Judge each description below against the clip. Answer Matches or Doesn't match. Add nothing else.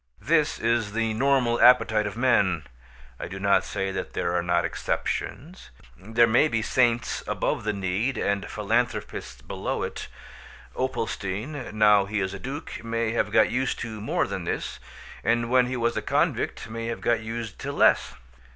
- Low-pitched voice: Matches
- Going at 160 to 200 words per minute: Matches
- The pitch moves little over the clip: Doesn't match